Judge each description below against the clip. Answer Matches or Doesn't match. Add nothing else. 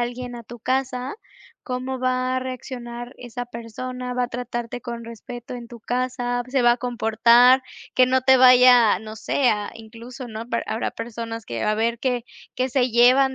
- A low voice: Doesn't match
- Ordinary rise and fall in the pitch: Doesn't match